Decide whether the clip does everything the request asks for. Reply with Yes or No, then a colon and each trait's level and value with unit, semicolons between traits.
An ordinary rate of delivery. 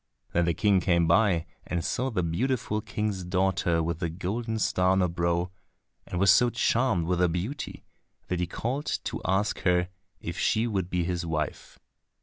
Yes: average, 180 wpm